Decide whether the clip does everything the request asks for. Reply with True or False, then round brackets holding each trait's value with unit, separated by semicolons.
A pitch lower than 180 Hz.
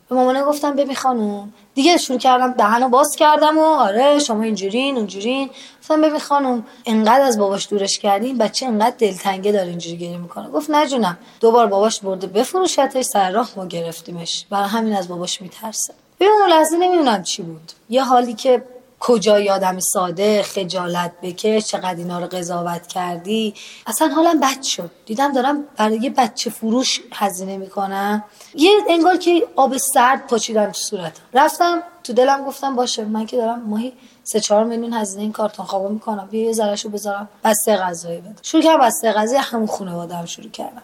False (225 Hz)